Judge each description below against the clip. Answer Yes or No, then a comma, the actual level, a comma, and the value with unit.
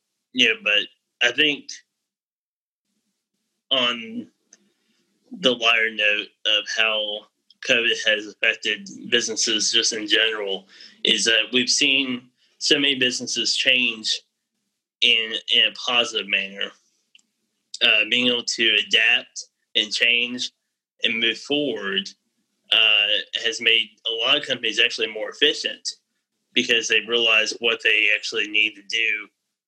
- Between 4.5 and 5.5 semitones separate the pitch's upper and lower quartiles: Yes, average, 5.2 semitones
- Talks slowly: Yes, slow, 120 wpm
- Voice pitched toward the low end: Yes, low, 120 Hz